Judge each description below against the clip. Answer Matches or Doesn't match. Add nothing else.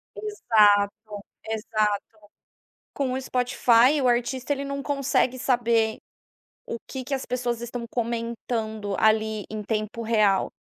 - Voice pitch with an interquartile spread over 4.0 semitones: Doesn't match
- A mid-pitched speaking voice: Doesn't match